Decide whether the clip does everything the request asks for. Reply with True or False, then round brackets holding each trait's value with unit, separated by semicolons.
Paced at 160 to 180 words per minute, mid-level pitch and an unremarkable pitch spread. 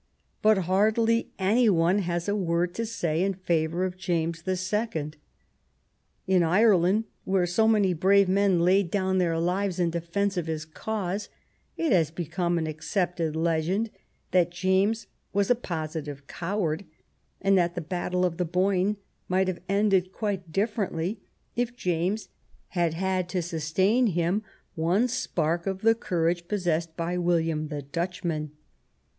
False (150 wpm; 180 Hz; 3.0 semitones)